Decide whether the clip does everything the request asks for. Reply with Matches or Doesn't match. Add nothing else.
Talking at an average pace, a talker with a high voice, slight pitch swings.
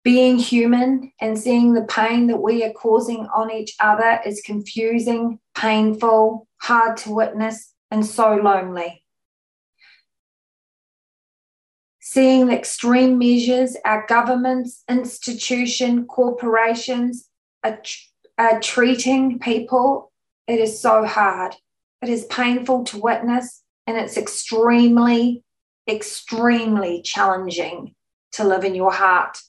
Doesn't match